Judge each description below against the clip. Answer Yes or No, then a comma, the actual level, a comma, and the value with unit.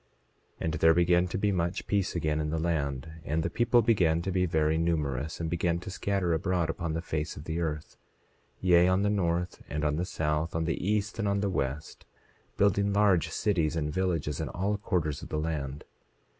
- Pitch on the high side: No, very low, 85 Hz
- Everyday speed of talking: No, fast, 210 wpm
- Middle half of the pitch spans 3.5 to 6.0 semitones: No, average, 3.1 semitones